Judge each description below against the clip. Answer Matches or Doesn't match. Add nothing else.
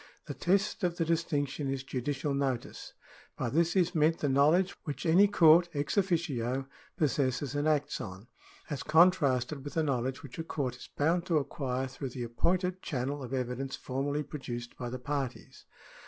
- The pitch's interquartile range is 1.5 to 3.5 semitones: Doesn't match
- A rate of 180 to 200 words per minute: Doesn't match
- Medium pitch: Matches